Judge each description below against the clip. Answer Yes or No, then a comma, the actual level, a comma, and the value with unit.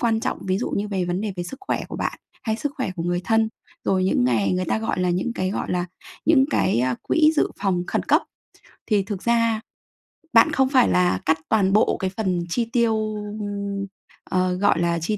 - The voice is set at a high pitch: Yes, high, 195 Hz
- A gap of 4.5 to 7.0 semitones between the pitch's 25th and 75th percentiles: No, average, 4.0 semitones